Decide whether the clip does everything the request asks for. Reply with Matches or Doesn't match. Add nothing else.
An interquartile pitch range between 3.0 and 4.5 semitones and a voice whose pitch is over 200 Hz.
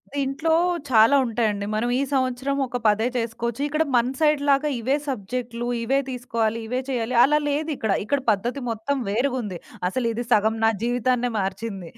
Matches